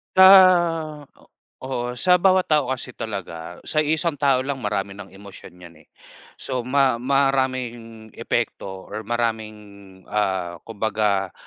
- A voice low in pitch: Yes, low, 120 Hz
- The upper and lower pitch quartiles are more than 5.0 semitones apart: Yes, wide, 5.6 semitones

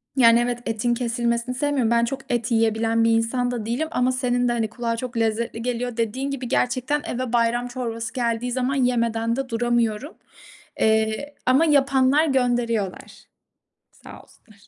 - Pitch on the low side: No, high, 240 Hz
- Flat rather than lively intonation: Yes, narrow, 1.9 semitones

